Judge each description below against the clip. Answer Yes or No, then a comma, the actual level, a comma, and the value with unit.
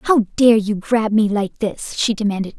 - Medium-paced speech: No, fast, 210 wpm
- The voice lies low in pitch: No, high, 215 Hz